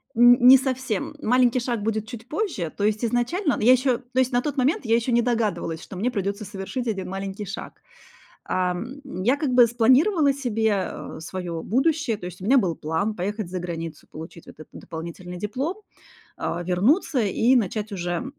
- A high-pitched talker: Yes, high, 225 Hz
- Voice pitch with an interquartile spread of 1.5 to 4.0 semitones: No, average, 5.2 semitones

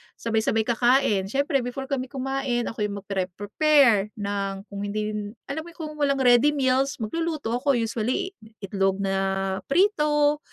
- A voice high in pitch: Yes, high, 240 Hz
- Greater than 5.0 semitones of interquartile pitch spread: Yes, wide, 5.5 semitones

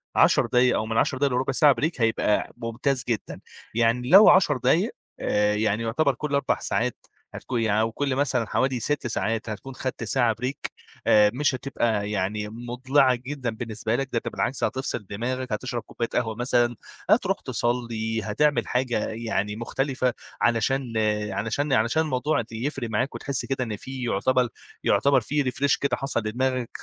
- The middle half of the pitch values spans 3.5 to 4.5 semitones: No, average, 3.0 semitones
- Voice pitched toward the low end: Yes, low, 125 Hz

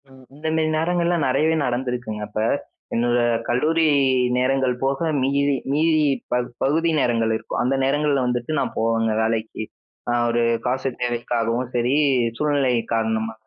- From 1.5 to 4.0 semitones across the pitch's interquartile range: Yes, average, 3.7 semitones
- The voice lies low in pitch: Yes, low, 130 Hz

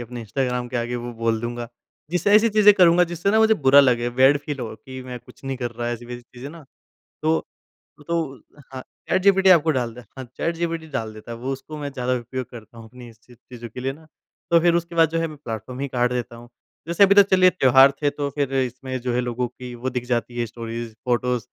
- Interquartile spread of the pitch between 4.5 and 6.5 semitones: Yes, average, 4.9 semitones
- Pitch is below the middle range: Yes, low, 130 Hz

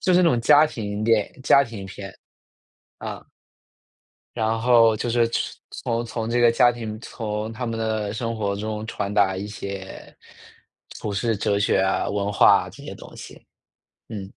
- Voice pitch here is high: No, low, 110 Hz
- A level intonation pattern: Yes, narrow, 2.3 semitones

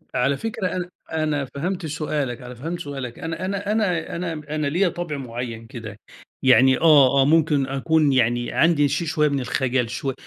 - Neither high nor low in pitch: Yes, medium, 145 Hz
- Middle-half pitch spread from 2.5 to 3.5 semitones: No, average, 4.0 semitones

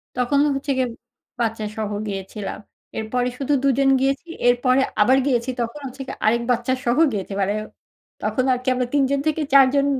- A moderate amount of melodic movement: Yes, average, 3.3 semitones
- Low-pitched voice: No, very high, 250 Hz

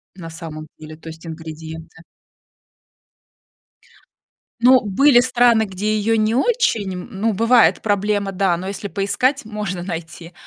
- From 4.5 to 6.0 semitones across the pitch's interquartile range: Yes, average, 5.2 semitones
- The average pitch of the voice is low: No, high, 200 Hz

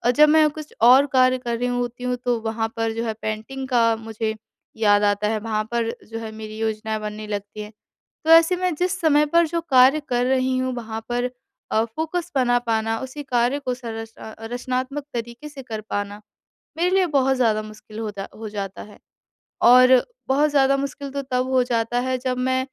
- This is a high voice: Yes, high, 245 Hz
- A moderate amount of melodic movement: Yes, average, 3.3 semitones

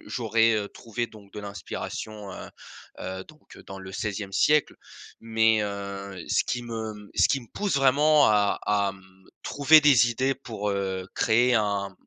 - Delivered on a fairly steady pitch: No, average, 3.5 semitones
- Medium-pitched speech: No, low, 110 Hz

